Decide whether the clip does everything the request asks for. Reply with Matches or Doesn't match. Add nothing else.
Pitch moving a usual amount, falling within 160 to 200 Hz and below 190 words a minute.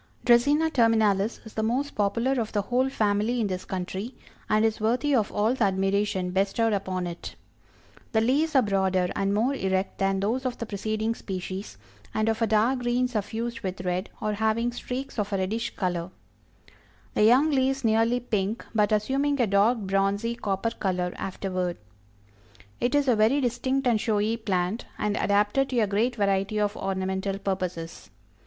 Doesn't match